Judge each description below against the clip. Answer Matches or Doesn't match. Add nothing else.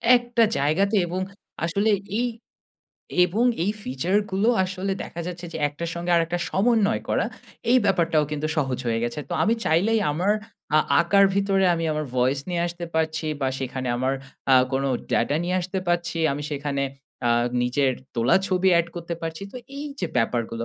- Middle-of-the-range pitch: Matches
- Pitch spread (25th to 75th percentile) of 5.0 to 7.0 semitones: Matches